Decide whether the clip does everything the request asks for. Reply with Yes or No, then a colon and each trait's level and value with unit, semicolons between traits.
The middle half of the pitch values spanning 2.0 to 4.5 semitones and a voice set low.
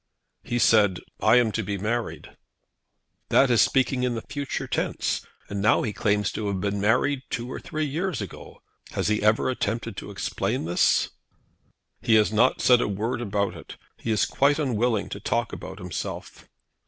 Yes: average, 3.5 semitones; low, 110 Hz